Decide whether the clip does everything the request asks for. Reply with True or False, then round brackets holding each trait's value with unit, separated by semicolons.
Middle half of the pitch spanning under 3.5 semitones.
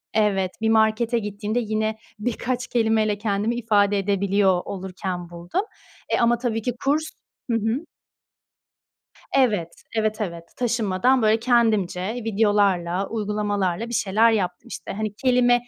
True (2.9 semitones)